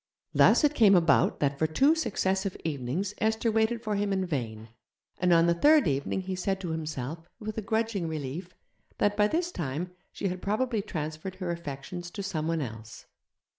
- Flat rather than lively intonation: No, average, 4.9 semitones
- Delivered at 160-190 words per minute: Yes, average, 180 wpm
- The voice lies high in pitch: No, medium, 180 Hz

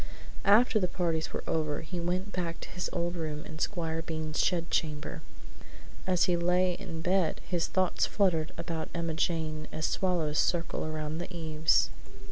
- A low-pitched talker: No, medium, 165 Hz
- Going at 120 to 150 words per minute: No, average, 165 wpm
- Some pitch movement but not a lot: No, narrow, 2.2 semitones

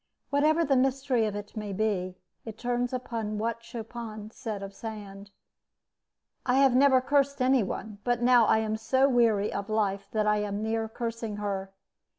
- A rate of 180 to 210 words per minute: No, average, 170 wpm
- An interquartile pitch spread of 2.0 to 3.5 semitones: Yes, average, 3.1 semitones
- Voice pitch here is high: Yes, high, 225 Hz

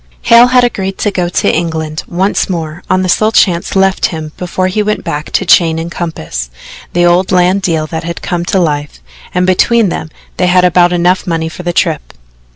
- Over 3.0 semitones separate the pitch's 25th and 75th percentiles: No, narrow, 2.6 semitones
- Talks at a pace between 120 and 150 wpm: No, fast, 205 wpm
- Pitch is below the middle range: No, medium, 175 Hz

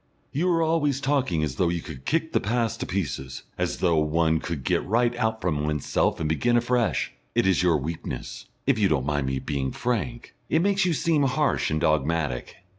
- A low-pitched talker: Yes, very low, 90 Hz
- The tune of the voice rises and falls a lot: Yes, wide, 8.9 semitones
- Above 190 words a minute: Yes, average, 200 wpm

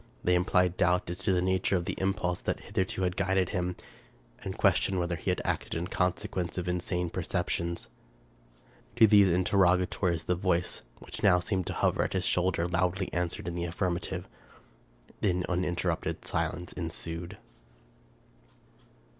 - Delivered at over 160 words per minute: No, average, 150 wpm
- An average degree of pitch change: No, narrow, 1.2 semitones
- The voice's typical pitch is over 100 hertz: No, very low, 90 Hz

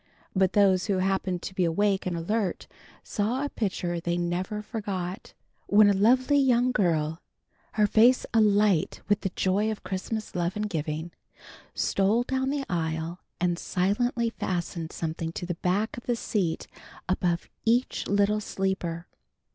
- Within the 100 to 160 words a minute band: Yes, average, 150 wpm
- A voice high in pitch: Yes, high, 195 Hz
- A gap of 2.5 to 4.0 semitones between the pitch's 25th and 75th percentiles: Yes, average, 3.7 semitones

